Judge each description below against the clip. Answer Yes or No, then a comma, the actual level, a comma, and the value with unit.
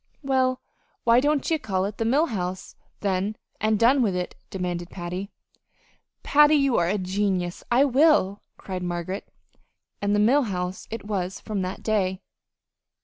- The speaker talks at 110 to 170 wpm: Yes, average, 150 wpm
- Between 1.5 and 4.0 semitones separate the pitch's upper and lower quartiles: No, average, 4.9 semitones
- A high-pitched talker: Yes, high, 205 Hz